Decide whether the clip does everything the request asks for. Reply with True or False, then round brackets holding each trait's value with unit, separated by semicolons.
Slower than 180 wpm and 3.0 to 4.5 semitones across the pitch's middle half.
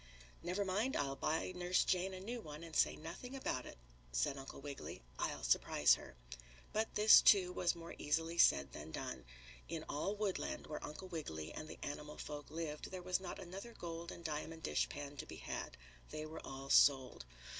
False (190 wpm; 4.1 semitones)